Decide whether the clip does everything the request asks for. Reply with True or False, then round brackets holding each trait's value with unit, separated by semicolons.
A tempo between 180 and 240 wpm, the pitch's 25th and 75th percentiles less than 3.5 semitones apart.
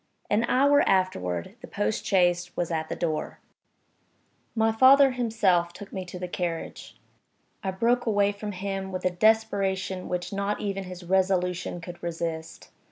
False (155 wpm; 2.8 semitones)